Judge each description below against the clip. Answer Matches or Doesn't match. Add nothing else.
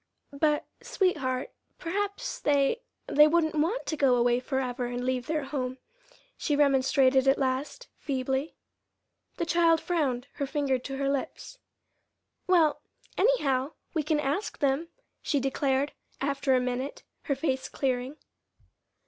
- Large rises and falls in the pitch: Doesn't match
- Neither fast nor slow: Doesn't match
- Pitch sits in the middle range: Doesn't match